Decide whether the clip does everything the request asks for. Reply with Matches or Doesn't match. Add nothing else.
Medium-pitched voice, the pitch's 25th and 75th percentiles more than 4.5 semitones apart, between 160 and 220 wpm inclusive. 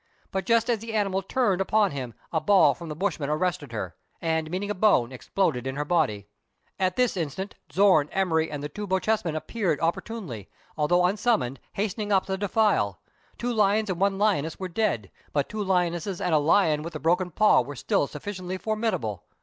Matches